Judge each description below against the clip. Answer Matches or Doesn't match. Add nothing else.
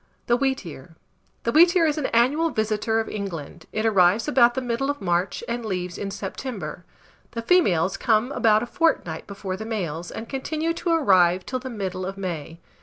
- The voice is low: Doesn't match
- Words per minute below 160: Doesn't match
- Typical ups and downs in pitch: Doesn't match